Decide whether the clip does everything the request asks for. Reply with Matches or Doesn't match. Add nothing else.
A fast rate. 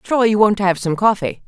Matches